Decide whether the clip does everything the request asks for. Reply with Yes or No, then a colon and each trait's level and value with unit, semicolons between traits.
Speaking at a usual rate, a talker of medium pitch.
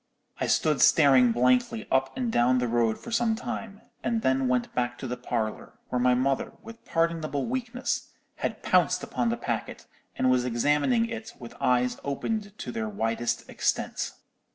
No: average, 170 wpm; low, 130 Hz